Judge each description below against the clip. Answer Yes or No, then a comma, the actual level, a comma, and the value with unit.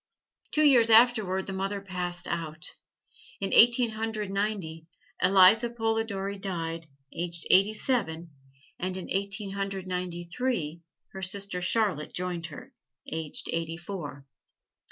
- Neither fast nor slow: No, slow, 125 wpm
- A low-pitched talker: No, high, 190 Hz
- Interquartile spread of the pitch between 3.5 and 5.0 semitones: Yes, average, 3.8 semitones